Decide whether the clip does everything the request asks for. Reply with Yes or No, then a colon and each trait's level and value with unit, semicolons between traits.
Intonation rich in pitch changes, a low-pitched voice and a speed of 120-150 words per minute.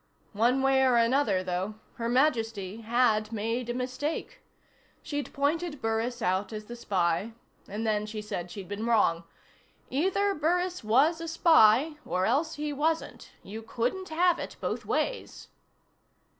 No: wide, 5.8 semitones; high, 240 Hz; average, 145 wpm